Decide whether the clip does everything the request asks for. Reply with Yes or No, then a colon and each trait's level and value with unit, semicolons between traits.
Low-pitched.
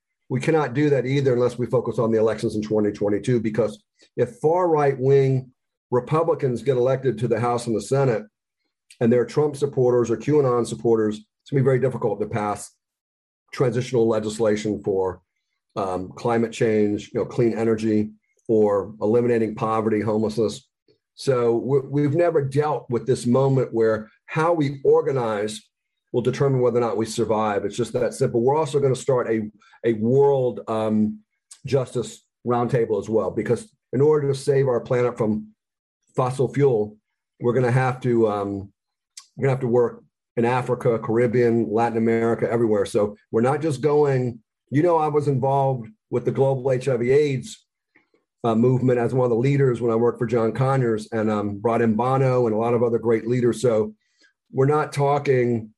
Yes: low, 120 Hz